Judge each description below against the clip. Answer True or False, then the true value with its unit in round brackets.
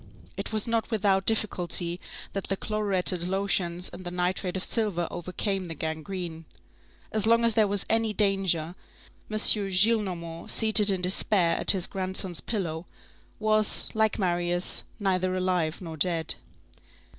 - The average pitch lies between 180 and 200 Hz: True (190 Hz)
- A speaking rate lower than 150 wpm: True (140 wpm)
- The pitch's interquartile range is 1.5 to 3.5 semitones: True (3.2 semitones)